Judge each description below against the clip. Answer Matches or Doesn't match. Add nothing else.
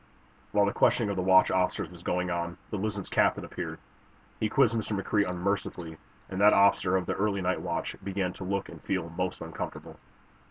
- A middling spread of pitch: Doesn't match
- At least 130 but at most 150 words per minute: Doesn't match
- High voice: Doesn't match